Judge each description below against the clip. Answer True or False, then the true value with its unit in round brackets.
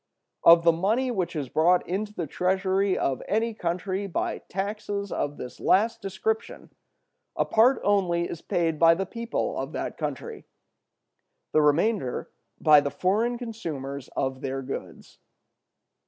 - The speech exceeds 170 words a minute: False (140 wpm)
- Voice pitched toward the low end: False (185 Hz)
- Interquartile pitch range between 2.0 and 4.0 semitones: False (4.8 semitones)